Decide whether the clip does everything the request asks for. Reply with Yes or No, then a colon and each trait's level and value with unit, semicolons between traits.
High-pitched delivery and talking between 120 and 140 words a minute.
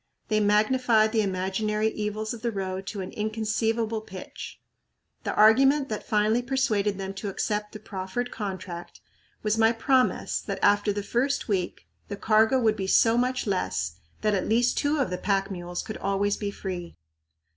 No: high, 215 Hz; average, 170 wpm